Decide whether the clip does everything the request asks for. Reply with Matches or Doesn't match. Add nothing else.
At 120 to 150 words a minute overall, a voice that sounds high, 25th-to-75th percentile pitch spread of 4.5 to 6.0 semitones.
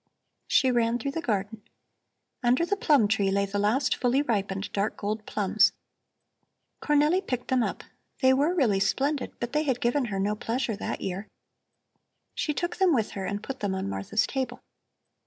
Doesn't match